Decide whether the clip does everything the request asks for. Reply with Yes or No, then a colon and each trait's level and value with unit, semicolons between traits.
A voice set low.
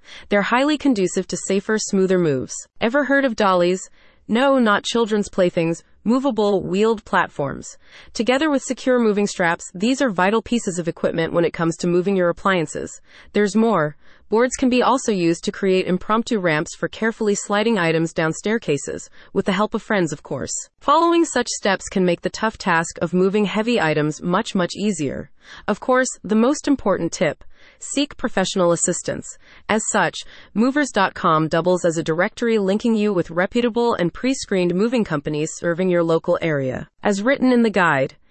No: high, 200 Hz